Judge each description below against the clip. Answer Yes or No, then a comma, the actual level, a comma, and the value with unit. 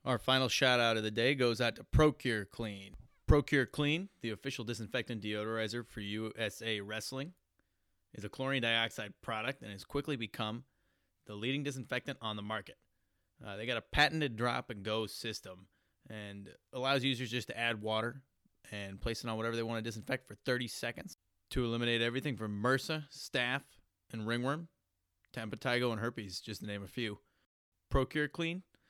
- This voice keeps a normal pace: Yes, average, 170 wpm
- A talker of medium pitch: No, low, 115 Hz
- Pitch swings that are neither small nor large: Yes, average, 3.6 semitones